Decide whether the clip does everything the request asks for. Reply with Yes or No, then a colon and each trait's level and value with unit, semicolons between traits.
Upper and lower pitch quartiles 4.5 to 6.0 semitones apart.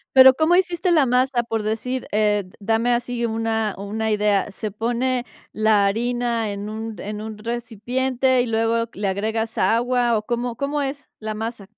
No: narrow, 2.4 semitones